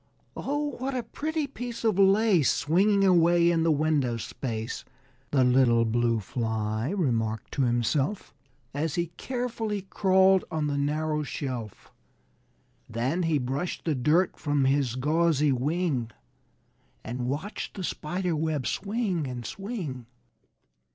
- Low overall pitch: No, medium, 155 Hz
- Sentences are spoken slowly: Yes, slow, 130 wpm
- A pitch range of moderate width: No, wide, 6.9 semitones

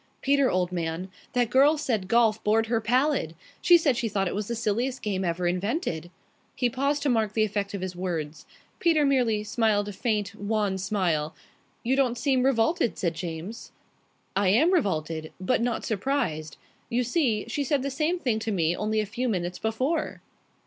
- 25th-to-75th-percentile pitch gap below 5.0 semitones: No, wide, 5.5 semitones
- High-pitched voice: Yes, high, 220 Hz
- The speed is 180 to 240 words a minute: Yes, average, 185 wpm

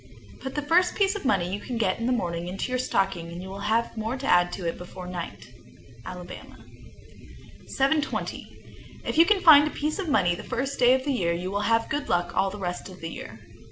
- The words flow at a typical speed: No, fast, 225 wpm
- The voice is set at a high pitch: Yes, high, 220 Hz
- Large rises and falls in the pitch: Yes, wide, 7.5 semitones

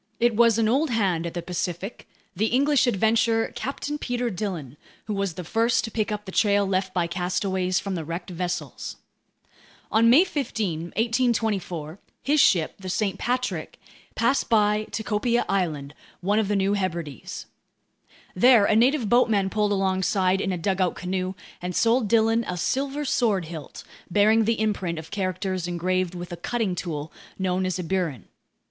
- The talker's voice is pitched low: No, high, 195 Hz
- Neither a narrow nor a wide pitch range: Yes, average, 4.0 semitones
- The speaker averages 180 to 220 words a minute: No, average, 165 wpm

